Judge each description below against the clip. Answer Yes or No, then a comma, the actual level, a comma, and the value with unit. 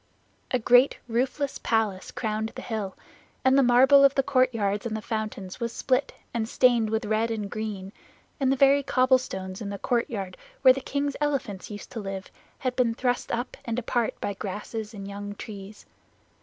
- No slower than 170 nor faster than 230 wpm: Yes, average, 180 wpm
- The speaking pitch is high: Yes, high, 230 Hz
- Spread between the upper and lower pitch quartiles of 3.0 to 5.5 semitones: Yes, average, 3.7 semitones